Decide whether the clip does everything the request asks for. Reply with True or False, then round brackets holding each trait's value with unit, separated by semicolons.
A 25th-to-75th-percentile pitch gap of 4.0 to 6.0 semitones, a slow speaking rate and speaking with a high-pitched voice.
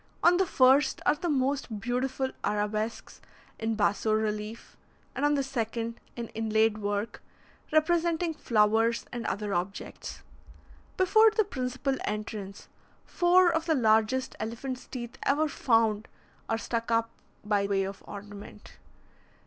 True (4.5 semitones; 130 wpm; 230 Hz)